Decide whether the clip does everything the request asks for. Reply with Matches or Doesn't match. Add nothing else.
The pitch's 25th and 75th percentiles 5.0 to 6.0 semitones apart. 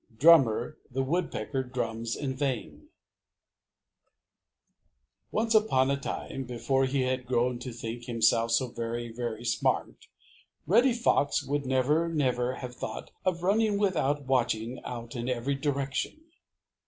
Doesn't match